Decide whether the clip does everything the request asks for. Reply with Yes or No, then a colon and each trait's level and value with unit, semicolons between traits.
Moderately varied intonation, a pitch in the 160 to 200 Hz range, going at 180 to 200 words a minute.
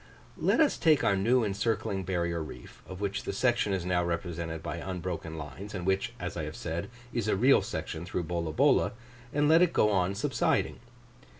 No: average, 4.1 semitones; very low, 95 Hz; average, 190 wpm